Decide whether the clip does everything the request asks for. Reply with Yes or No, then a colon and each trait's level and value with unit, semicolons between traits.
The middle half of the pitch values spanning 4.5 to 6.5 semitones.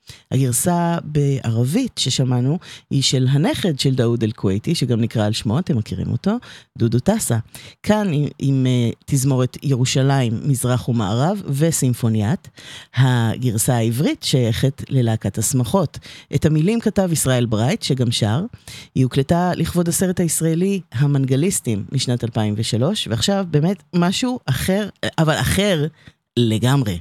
Yes: wide, 5.6 semitones